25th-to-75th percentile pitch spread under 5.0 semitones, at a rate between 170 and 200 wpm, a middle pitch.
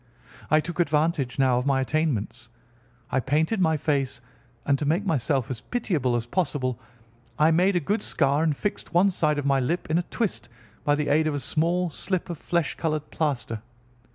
Yes: average, 3.8 semitones; average, 190 wpm; medium, 155 Hz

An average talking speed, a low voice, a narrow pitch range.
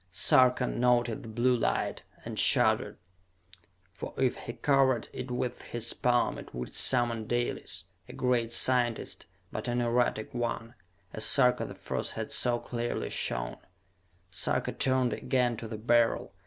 Yes: average, 145 wpm; low, 120 Hz; narrow, 1.4 semitones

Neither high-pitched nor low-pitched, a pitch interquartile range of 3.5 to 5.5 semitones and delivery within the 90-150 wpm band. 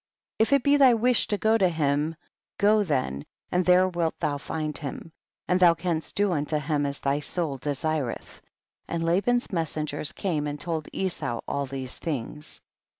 No: medium, 160 Hz; average, 4.2 semitones; average, 180 wpm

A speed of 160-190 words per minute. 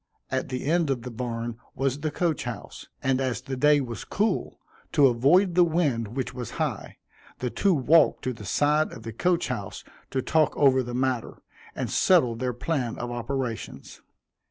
Yes: average, 180 wpm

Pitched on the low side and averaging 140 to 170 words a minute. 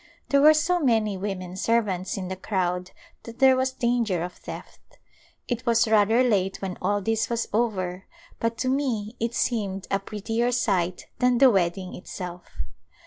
No: high, 215 Hz; average, 165 wpm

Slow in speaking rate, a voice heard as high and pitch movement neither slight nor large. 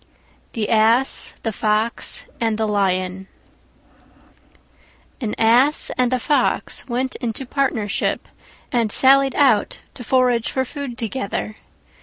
Yes: slow, 115 wpm; high, 235 Hz; average, 3.4 semitones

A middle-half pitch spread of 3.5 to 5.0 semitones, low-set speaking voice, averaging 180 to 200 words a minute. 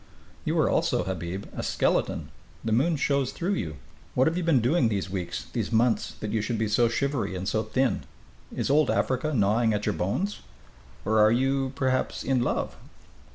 Yes: average, 4.3 semitones; low, 120 Hz; average, 195 wpm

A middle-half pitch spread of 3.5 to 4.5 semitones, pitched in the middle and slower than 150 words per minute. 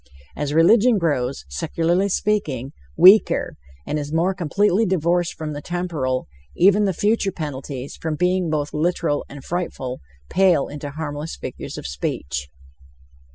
Yes: average, 4.1 semitones; medium, 160 Hz; slow, 135 wpm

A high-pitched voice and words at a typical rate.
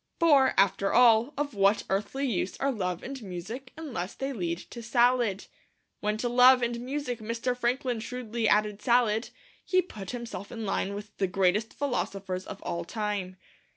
Yes: high, 225 Hz; average, 165 wpm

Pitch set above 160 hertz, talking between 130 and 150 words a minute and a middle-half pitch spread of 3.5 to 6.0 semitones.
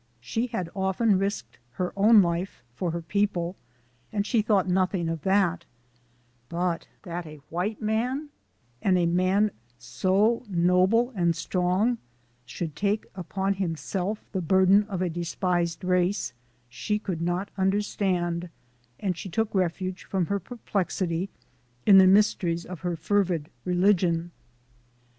No: medium, 185 Hz; average, 140 wpm; average, 2.8 semitones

